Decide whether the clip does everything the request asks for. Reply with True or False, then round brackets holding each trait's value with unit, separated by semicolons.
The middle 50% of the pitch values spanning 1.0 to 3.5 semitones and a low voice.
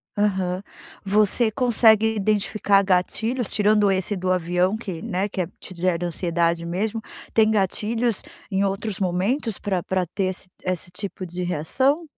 False (3.0 semitones; 195 Hz)